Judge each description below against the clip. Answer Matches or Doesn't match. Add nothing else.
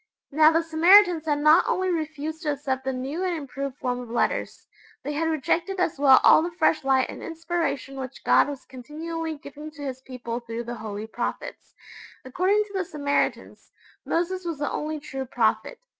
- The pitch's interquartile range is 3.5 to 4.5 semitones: Matches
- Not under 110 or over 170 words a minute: Doesn't match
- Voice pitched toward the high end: Matches